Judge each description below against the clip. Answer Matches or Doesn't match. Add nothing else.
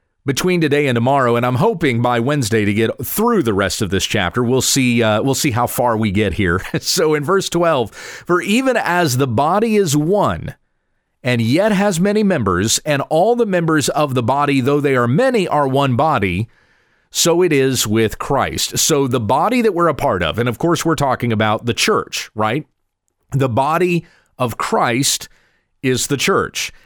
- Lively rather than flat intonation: Matches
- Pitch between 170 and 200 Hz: Doesn't match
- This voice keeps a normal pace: Matches